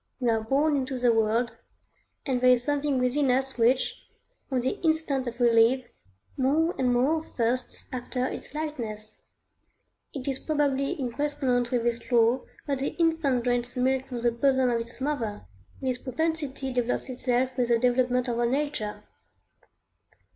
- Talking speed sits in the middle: Yes, average, 160 wpm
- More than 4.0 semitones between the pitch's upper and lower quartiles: No, narrow, 2.4 semitones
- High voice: Yes, very high, 255 Hz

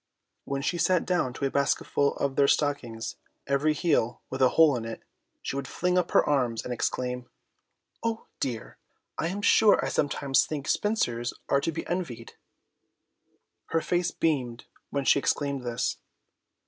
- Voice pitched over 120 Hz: Yes, medium, 140 Hz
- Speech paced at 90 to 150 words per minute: No, average, 160 wpm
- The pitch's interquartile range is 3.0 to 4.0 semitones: No, average, 4.7 semitones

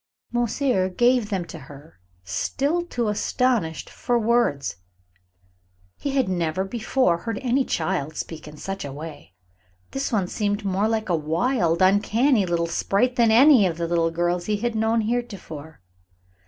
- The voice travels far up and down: Yes, wide, 6.2 semitones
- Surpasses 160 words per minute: No, average, 155 wpm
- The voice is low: No, high, 200 Hz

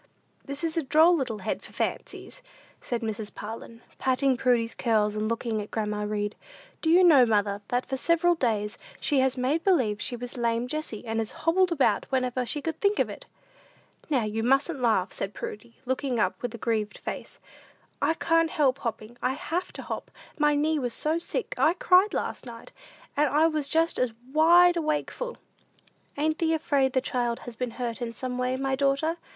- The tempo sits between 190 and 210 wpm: Yes, average, 195 wpm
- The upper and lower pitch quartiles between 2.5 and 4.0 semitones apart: No, average, 5.3 semitones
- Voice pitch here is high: Yes, very high, 260 Hz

